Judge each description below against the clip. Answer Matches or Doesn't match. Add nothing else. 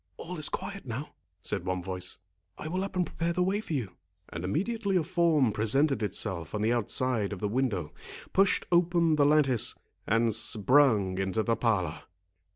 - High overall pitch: Doesn't match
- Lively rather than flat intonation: Matches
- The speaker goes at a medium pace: Matches